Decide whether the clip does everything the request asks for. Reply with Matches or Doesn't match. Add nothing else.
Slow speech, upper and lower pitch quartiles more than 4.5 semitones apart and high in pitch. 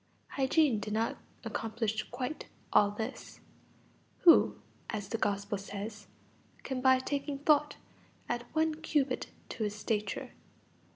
Matches